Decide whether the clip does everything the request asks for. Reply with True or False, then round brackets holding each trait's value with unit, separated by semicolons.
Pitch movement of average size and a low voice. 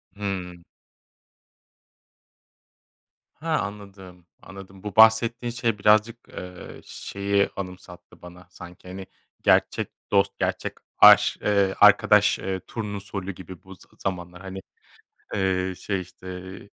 False (1.9 semitones; 95 Hz)